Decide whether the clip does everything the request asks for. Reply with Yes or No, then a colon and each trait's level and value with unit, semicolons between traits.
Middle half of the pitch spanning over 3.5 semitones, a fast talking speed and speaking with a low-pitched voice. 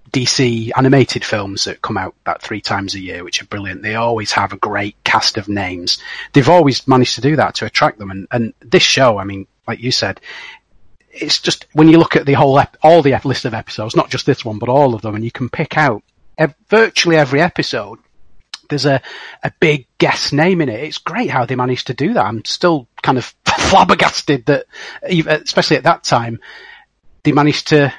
Yes: average, 5.2 semitones; fast, 215 wpm; low, 130 Hz